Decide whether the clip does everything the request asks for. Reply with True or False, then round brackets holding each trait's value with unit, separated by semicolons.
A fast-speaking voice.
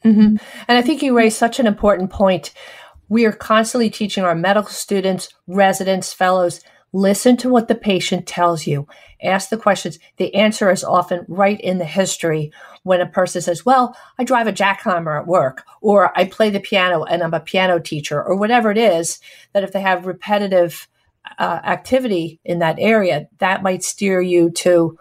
False (185 wpm)